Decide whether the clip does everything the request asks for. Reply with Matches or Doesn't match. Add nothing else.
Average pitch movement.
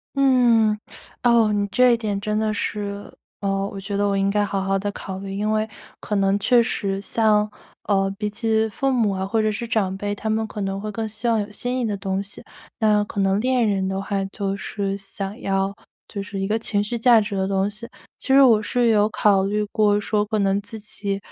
Doesn't match